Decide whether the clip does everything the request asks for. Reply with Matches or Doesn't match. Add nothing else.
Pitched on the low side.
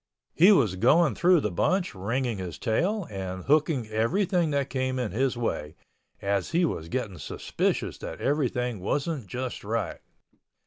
Matches